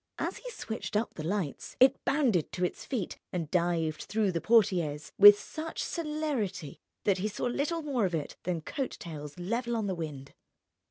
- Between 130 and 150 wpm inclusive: No, average, 180 wpm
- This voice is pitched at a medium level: No, high, 200 Hz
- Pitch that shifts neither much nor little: No, wide, 6.6 semitones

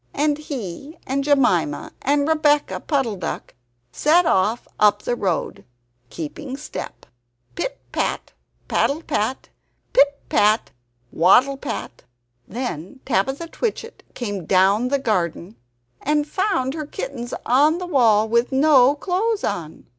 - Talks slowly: Yes, slow, 125 wpm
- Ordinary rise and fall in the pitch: No, wide, 6.1 semitones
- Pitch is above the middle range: Yes, very high, 265 Hz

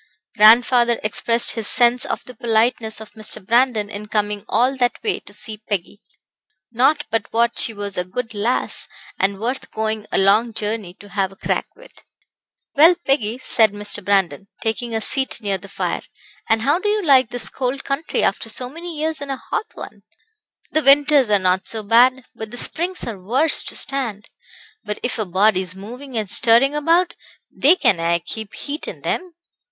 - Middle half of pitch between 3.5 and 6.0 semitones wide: Yes, average, 4.5 semitones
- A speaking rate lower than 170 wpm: No, average, 185 wpm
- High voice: Yes, high, 230 Hz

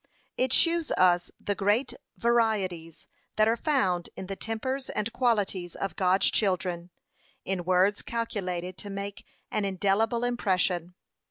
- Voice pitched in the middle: No, high, 200 Hz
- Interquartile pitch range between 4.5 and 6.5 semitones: No, average, 4.0 semitones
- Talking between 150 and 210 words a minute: No, slow, 135 wpm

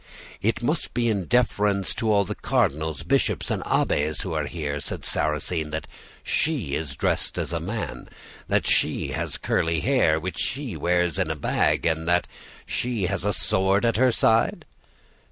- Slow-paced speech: No, average, 170 wpm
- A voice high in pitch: No, very low, 95 Hz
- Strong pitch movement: Yes, wide, 6.1 semitones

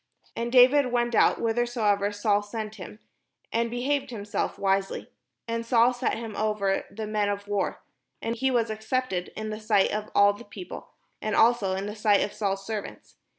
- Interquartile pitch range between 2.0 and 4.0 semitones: Yes, average, 2.7 semitones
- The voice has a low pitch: No, high, 215 Hz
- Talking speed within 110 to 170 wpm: No, average, 185 wpm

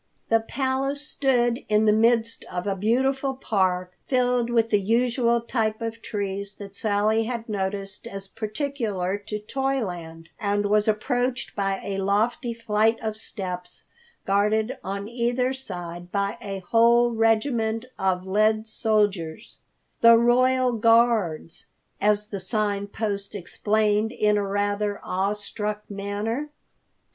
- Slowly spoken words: Yes, slow, 130 wpm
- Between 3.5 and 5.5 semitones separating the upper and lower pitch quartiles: No, average, 2.8 semitones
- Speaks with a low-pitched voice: No, high, 215 Hz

